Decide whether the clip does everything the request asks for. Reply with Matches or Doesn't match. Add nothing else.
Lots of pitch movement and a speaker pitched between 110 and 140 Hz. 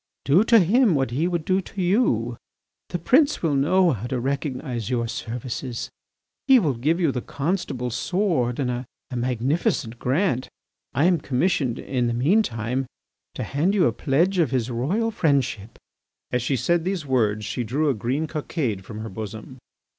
Matches